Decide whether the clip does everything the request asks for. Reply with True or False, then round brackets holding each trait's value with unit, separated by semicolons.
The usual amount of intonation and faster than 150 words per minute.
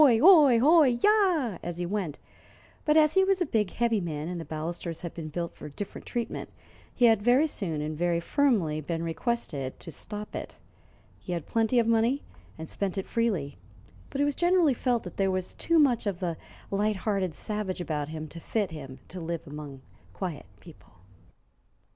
False (6.7 semitones; 190 wpm)